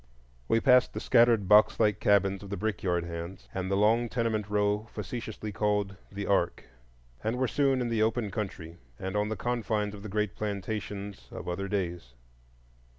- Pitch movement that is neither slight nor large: No, narrow, 2.2 semitones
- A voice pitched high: No, low, 105 Hz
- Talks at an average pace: Yes, average, 175 wpm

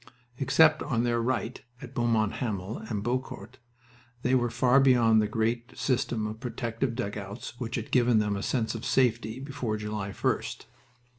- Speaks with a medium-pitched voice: No, low, 115 Hz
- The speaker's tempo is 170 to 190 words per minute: No, average, 160 wpm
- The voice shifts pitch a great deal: No, narrow, 2.4 semitones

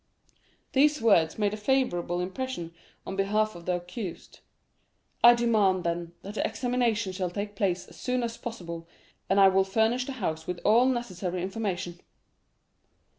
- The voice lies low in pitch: No, high, 200 Hz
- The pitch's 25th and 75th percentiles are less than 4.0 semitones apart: No, average, 4.8 semitones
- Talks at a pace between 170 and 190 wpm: No, average, 155 wpm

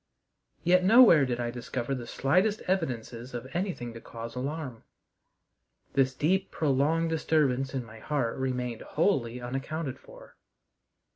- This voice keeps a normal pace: No, slow, 130 wpm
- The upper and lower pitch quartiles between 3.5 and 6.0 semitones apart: Yes, average, 5.0 semitones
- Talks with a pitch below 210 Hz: Yes, low, 135 Hz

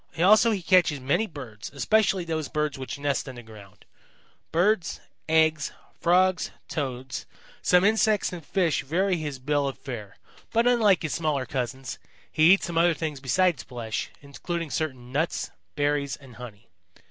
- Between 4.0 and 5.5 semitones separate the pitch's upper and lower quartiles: Yes, average, 5.1 semitones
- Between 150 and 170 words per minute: Yes, average, 155 wpm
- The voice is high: No, medium, 150 Hz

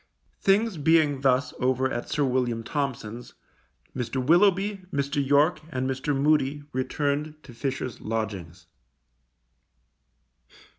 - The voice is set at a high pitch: No, low, 135 Hz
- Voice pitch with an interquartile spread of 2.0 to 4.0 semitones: Yes, average, 3.1 semitones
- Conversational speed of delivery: No, slow, 105 wpm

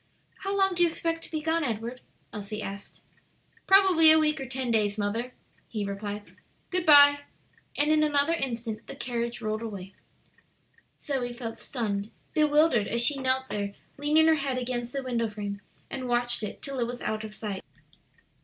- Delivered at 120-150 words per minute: No, average, 175 wpm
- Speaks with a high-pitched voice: Yes, high, 245 Hz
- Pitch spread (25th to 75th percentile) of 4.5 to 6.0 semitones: Yes, wide, 5.6 semitones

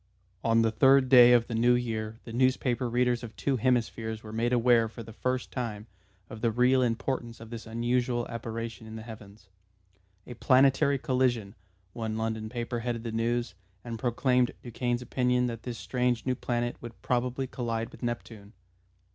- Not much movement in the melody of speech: Yes, narrow, 1.7 semitones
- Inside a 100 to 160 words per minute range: No, average, 170 wpm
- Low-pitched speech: Yes, low, 120 Hz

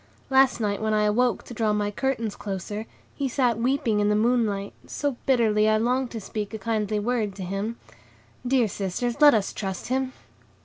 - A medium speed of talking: Yes, average, 185 wpm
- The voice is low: No, high, 220 Hz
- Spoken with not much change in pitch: No, average, 3.1 semitones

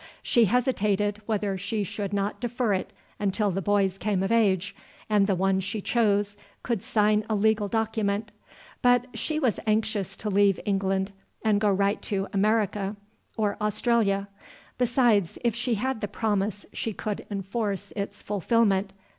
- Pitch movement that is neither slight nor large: No, narrow, 2.1 semitones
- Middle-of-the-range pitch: No, high, 205 Hz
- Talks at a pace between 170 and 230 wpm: No, average, 155 wpm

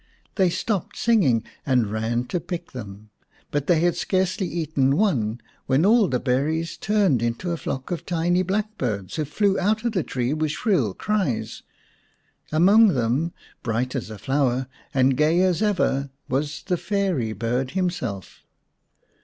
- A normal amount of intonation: No, wide, 6.8 semitones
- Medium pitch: Yes, medium, 155 Hz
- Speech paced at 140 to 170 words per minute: Yes, average, 155 wpm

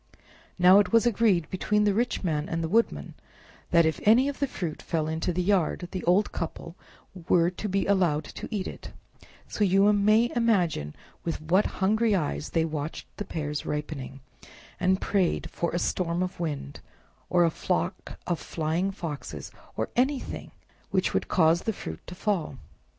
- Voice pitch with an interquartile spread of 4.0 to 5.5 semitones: Yes, average, 4.3 semitones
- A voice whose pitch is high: No, medium, 180 Hz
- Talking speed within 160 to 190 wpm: Yes, average, 170 wpm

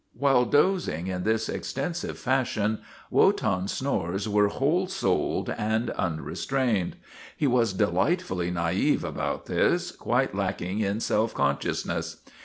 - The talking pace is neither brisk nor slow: No, slow, 115 wpm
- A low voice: Yes, low, 110 Hz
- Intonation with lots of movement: Yes, wide, 6.5 semitones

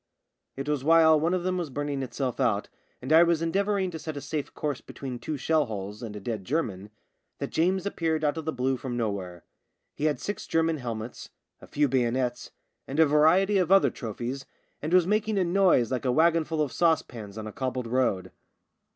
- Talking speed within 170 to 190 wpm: No, fast, 205 wpm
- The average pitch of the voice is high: No, medium, 145 Hz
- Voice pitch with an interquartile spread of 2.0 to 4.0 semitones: No, average, 5.1 semitones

